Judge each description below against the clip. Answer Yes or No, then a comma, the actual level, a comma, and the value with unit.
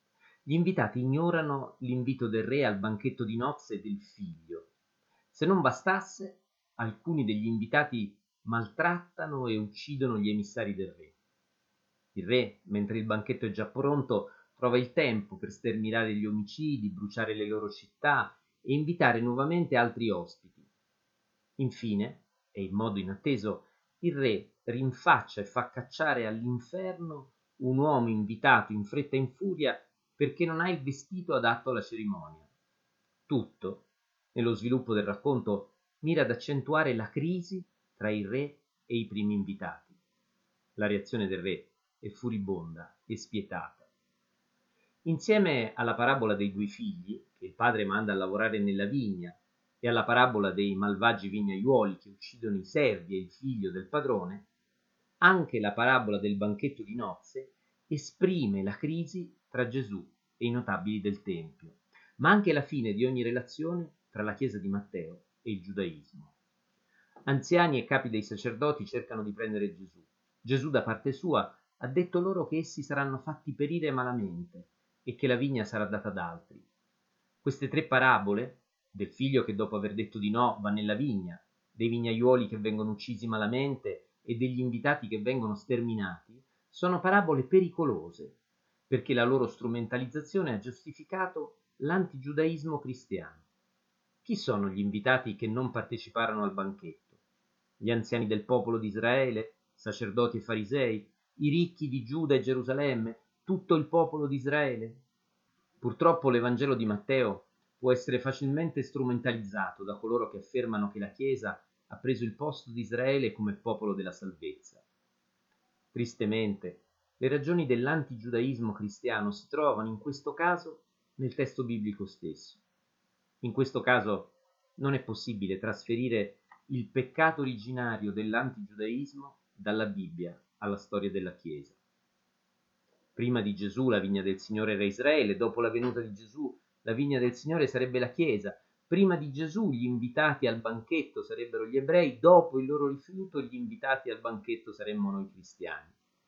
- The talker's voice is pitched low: Yes, low, 125 Hz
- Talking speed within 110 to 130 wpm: No, average, 145 wpm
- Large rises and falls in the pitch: Yes, wide, 6.3 semitones